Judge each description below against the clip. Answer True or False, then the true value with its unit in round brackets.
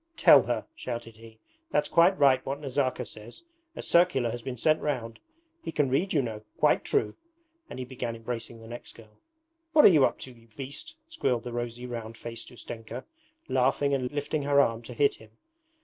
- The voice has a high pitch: False (125 Hz)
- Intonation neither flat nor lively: True (3.6 semitones)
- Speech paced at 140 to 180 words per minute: False (195 wpm)